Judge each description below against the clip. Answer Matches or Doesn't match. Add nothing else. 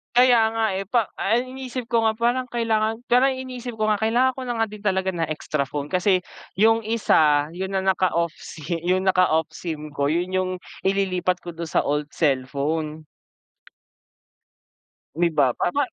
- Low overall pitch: Doesn't match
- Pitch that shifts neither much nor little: Doesn't match